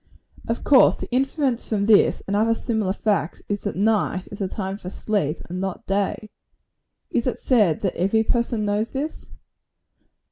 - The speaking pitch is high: Yes, high, 210 Hz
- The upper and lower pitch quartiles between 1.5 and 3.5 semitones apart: Yes, average, 2.9 semitones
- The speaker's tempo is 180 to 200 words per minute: No, average, 170 wpm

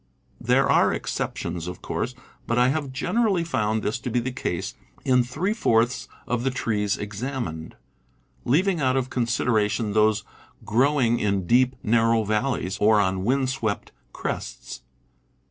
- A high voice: No, low, 120 Hz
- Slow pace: No, average, 145 wpm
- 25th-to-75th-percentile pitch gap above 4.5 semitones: No, average, 3.7 semitones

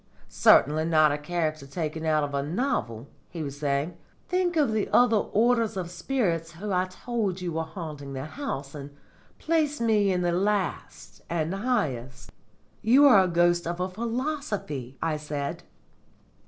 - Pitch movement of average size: No, wide, 6.3 semitones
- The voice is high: No, medium, 175 Hz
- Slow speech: No, average, 160 wpm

